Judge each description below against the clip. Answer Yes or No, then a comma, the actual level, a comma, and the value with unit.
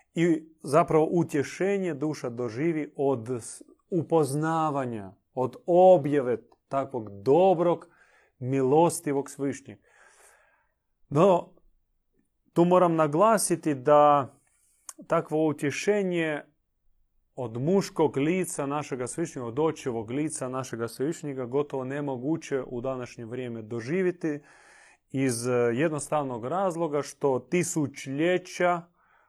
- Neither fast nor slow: No, slow, 85 wpm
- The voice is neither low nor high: Yes, medium, 145 Hz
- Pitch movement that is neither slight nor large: Yes, average, 4.5 semitones